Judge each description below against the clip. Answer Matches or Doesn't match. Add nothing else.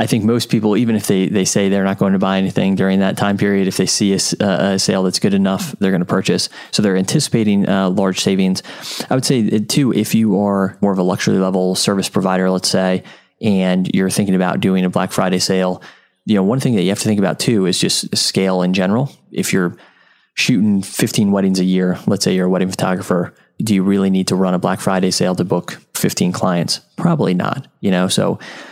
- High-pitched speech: Doesn't match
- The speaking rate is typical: Doesn't match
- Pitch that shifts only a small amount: Matches